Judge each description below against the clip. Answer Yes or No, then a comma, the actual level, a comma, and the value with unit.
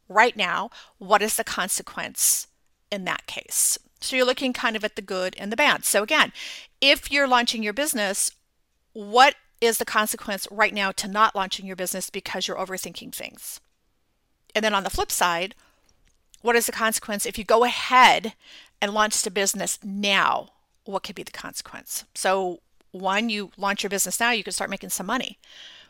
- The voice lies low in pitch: No, high, 215 Hz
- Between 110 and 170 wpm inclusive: No, average, 185 wpm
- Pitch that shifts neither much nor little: Yes, average, 3.4 semitones